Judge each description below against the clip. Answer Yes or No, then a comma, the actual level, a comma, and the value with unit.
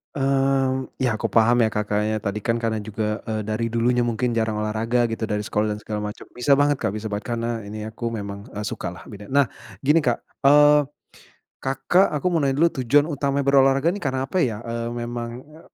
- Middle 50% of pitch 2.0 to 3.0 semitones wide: No, average, 4.1 semitones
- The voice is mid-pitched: No, low, 120 Hz